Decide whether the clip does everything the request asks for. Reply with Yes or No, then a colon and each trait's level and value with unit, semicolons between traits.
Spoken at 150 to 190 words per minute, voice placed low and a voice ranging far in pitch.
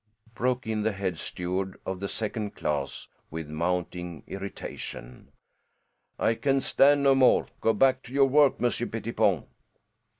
No: average, 140 wpm; low, 105 Hz; wide, 6.4 semitones